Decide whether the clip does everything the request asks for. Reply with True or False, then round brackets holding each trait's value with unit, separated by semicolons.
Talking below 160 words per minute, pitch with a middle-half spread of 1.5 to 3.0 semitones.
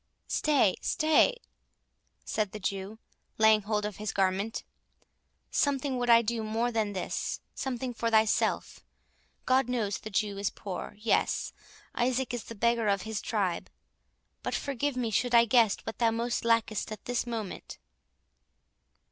True (140 wpm; 2.6 semitones)